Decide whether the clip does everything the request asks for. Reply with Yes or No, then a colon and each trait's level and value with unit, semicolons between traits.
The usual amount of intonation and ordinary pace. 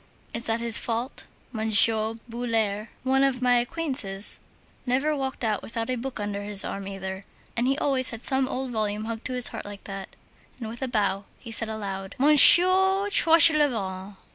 Yes: average, 4.2 semitones; average, 175 wpm